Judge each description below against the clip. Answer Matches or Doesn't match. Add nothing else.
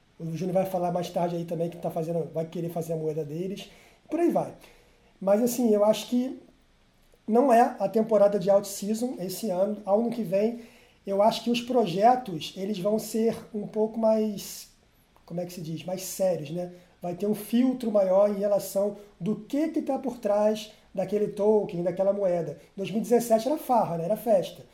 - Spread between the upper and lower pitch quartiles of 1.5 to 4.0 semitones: Matches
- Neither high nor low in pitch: Doesn't match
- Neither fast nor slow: Doesn't match